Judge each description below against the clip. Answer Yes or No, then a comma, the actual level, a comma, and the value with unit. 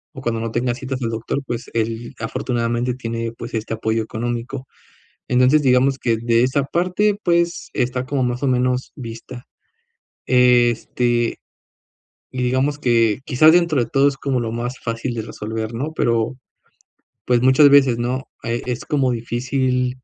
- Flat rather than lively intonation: Yes, narrow, 2.2 semitones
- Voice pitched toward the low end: Yes, low, 125 Hz